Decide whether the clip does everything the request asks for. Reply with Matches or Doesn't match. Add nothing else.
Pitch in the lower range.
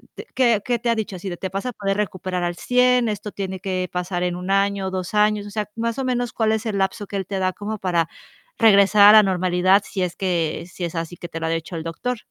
Doesn't match